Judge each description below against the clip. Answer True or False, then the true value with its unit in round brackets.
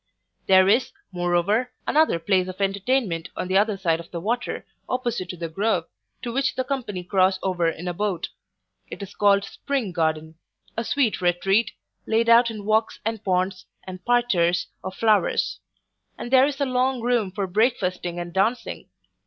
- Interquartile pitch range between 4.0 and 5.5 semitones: True (4.6 semitones)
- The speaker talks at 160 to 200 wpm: True (170 wpm)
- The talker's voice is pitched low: False (200 Hz)